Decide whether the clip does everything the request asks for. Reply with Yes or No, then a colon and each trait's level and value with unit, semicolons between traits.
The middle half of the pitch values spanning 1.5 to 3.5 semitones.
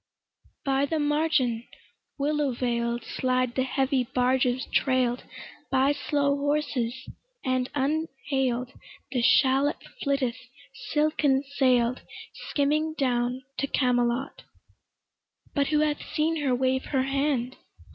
Yes: narrow, 2.4 semitones